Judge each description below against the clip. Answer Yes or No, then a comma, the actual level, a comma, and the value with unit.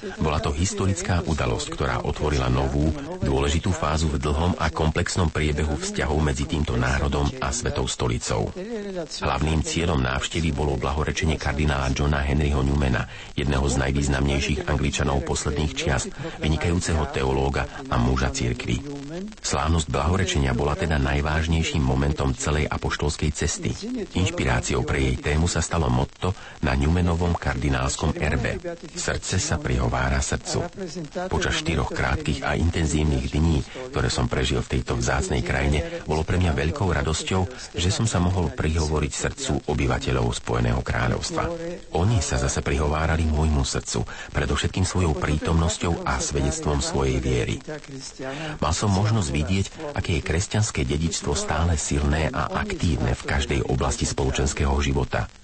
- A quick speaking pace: No, average, 135 wpm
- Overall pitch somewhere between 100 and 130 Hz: No, very low, 75 Hz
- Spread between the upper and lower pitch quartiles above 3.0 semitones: Yes, average, 3.9 semitones